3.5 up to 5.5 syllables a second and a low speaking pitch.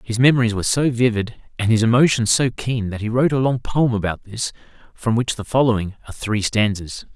No: 5.9 syllables/s; low, 115 Hz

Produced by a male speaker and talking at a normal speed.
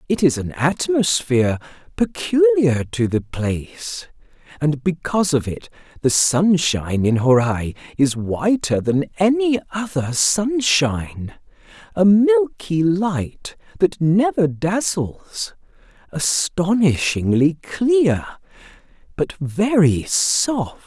No: male; slow, 90 wpm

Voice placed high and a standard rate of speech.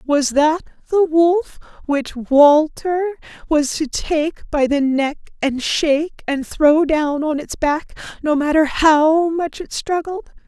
Yes: very high, 305 Hz; average, 150 wpm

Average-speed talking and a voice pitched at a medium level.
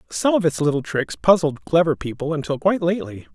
Yes: average, 195 wpm; medium, 160 Hz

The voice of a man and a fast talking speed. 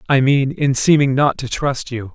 Yes: male; fast, 225 wpm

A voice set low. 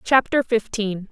No: high, 225 Hz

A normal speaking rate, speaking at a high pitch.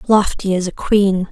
Yes: average, 185 wpm; high, 195 Hz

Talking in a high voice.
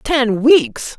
Yes: very high, 270 Hz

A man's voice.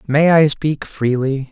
Yes: male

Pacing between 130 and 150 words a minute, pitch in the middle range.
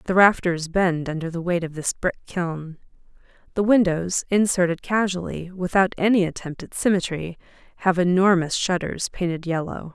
Yes: average, 145 wpm; medium, 180 Hz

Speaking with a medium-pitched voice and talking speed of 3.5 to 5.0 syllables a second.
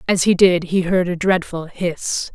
Yes: medium, 175 Hz; 4.1 syllables/s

